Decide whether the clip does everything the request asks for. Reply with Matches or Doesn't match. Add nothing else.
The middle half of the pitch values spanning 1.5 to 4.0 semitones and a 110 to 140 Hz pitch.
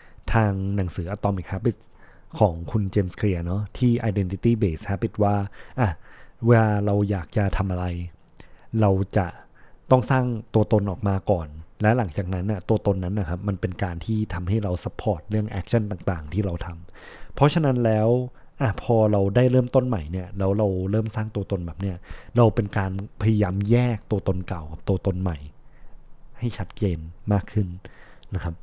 Doesn't match